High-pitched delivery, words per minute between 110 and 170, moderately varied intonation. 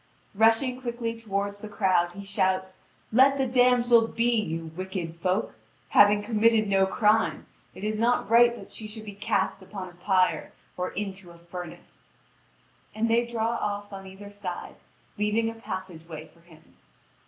Yes: high, 205 Hz; average, 165 wpm; average, 3.4 semitones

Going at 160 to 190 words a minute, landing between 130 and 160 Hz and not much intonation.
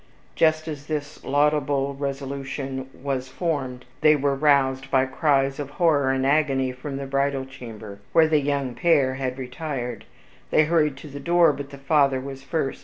Yes: average, 170 wpm; medium, 140 Hz; narrow, 1.9 semitones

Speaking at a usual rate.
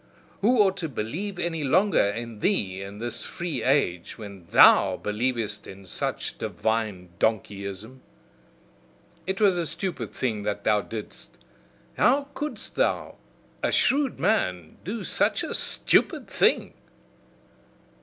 No: slow, 125 wpm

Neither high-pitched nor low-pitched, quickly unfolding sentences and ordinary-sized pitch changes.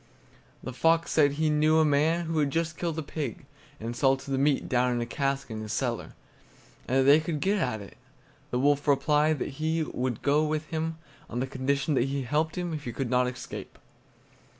Yes: medium, 145 Hz; fast, 210 wpm; average, 3.2 semitones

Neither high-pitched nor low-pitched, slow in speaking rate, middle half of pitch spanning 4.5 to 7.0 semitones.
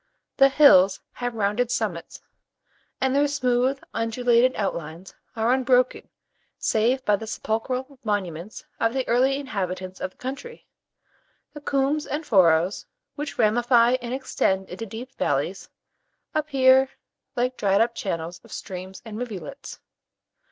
No: high, 235 Hz; slow, 130 wpm; average, 4.8 semitones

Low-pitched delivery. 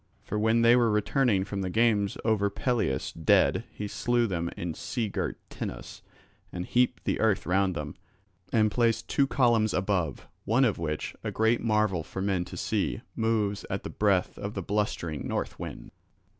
Yes: low, 105 Hz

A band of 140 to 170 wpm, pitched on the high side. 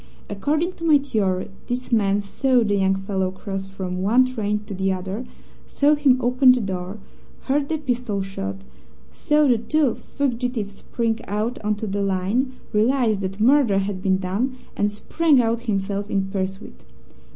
Yes: average, 165 wpm; high, 210 Hz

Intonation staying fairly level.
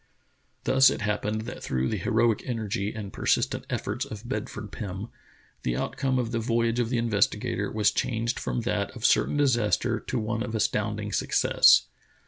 Yes: narrow, 2.2 semitones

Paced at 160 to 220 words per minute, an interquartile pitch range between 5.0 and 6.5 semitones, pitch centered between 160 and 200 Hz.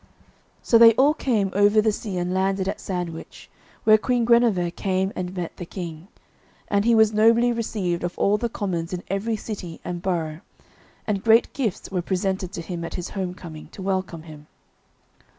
No: average, 180 wpm; average, 3.6 semitones; high, 190 Hz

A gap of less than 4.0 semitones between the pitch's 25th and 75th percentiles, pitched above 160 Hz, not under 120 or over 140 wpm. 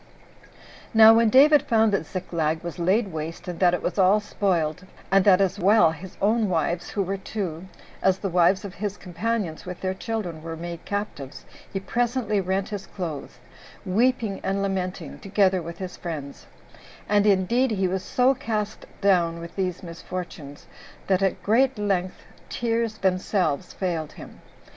No: average, 3.3 semitones; high, 190 Hz; average, 160 wpm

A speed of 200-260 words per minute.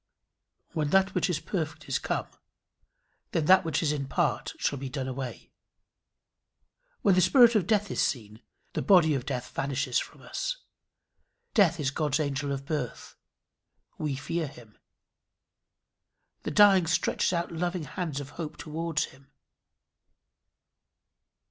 No: average, 140 wpm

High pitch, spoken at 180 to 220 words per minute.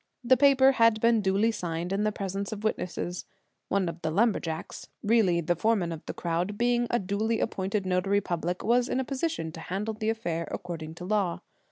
Yes: high, 200 Hz; average, 195 wpm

